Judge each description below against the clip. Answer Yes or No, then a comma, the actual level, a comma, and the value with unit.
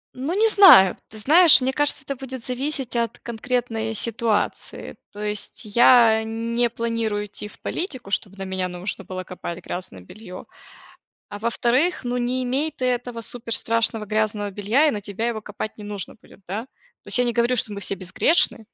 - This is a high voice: Yes, high, 230 Hz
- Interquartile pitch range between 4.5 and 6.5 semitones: No, average, 3.3 semitones